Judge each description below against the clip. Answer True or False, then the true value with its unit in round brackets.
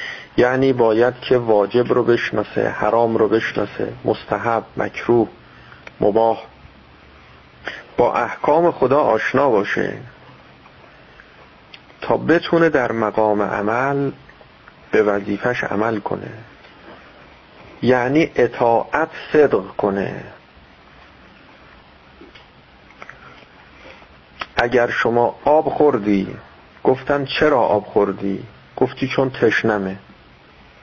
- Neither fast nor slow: False (80 wpm)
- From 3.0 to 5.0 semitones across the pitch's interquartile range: True (3.8 semitones)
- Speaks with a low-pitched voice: True (115 Hz)